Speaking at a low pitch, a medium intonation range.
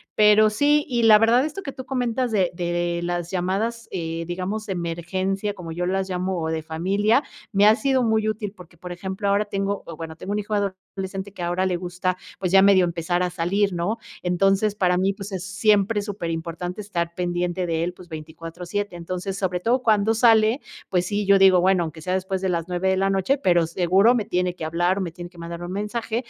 No: high, 190 Hz; average, 3.0 semitones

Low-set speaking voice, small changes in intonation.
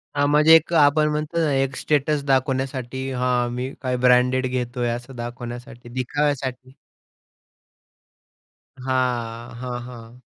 Yes: low, 130 Hz; narrow, 2.3 semitones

